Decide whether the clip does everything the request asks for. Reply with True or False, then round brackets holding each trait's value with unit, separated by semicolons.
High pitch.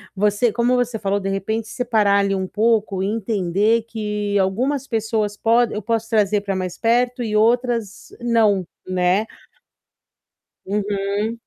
True (215 Hz)